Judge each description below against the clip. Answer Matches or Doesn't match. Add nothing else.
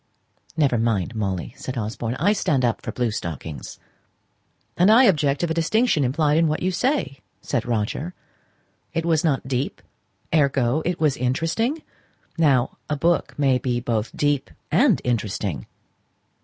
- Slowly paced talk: Doesn't match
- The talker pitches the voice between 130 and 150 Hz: Matches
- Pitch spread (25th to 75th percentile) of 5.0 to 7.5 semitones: Matches